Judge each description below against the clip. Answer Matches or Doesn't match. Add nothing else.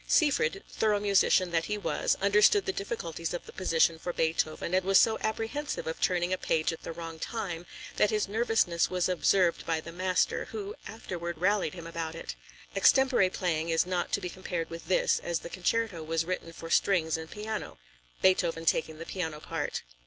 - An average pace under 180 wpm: Doesn't match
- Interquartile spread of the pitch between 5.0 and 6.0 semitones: Doesn't match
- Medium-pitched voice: Matches